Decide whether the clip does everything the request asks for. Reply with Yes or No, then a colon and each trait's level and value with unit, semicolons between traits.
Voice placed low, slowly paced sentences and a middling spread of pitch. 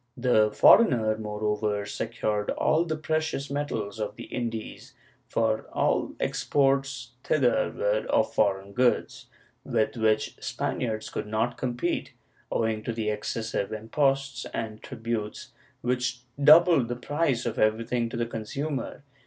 Yes: low, 115 Hz; slow, 130 wpm; average, 4.0 semitones